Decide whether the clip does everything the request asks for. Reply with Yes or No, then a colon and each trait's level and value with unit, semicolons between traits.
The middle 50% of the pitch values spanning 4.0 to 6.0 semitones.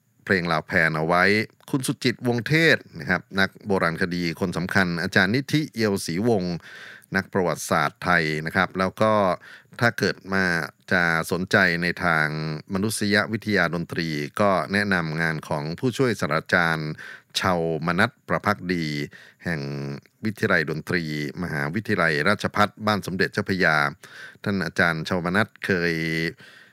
Yes: average, 4.5 semitones